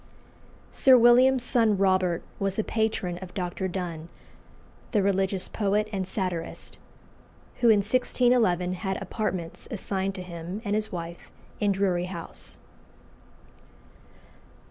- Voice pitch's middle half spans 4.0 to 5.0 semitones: No, average, 3.1 semitones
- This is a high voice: Yes, high, 195 Hz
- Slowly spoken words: Yes, slow, 120 wpm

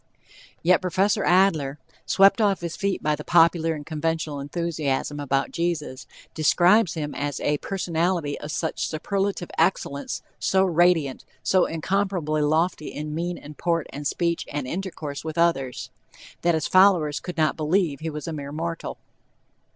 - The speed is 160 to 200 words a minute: No, average, 150 wpm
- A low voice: No, medium, 165 Hz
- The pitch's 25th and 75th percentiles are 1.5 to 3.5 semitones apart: Yes, average, 3.2 semitones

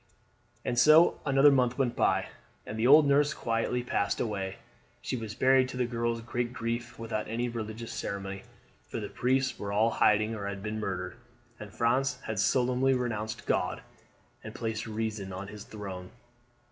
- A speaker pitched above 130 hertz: No, low, 115 Hz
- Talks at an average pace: Yes, average, 175 wpm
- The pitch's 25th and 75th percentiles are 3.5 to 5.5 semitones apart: No, average, 2.9 semitones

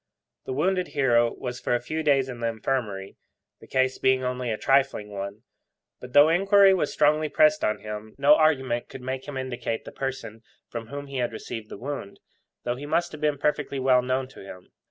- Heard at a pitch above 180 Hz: No, low, 130 Hz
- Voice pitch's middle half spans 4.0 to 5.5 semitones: No, average, 3.6 semitones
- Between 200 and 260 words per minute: Yes, fast, 205 wpm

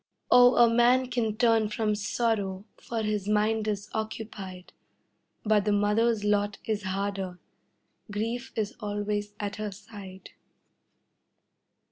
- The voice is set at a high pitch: Yes, high, 210 Hz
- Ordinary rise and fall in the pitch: No, narrow, 1.7 semitones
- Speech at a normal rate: No, slow, 120 wpm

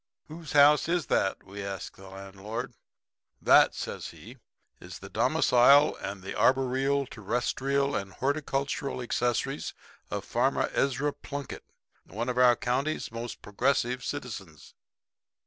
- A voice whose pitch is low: Yes, low, 125 Hz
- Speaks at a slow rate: Yes, slow, 125 wpm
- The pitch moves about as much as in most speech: Yes, average, 4.3 semitones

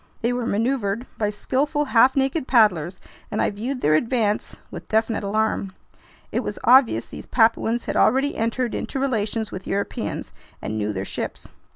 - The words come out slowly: No, average, 165 wpm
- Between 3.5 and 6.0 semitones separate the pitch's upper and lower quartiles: Yes, average, 4.1 semitones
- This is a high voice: Yes, high, 225 Hz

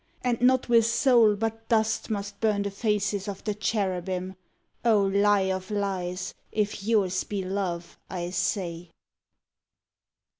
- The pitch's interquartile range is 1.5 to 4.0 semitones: Yes, narrow, 2.6 semitones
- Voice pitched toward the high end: Yes, high, 200 Hz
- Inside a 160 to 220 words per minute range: No, slow, 135 wpm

